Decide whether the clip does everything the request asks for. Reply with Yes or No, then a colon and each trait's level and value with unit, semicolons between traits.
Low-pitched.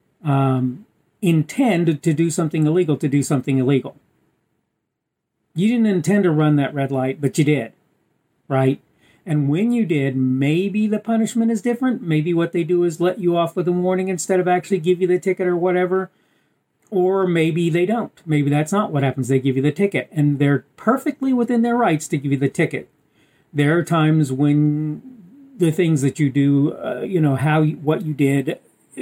No: medium, 165 Hz